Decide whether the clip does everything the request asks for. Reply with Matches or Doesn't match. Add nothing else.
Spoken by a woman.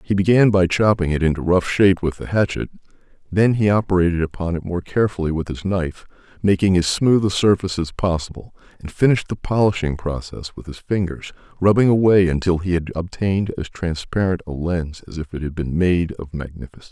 Doesn't match